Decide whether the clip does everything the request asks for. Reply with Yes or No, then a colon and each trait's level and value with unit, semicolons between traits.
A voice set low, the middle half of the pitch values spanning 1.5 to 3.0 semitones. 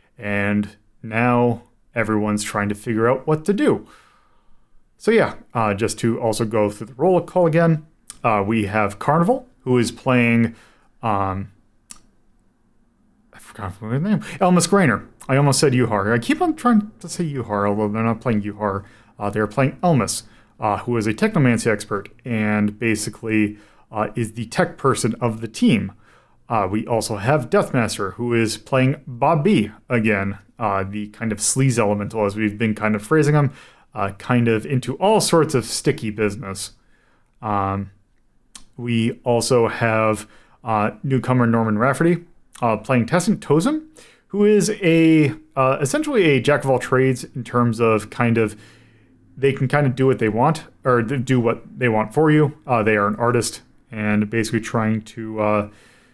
No: low, 115 Hz; average, 4.3 semitones